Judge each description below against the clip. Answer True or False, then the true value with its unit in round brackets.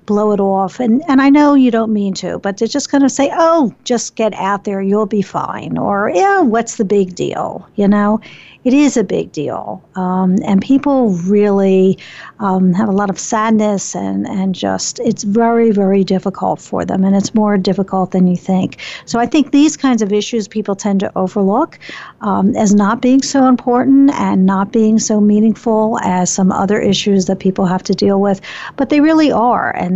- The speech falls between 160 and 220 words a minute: True (200 wpm)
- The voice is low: False (210 Hz)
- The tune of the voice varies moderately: True (3.4 semitones)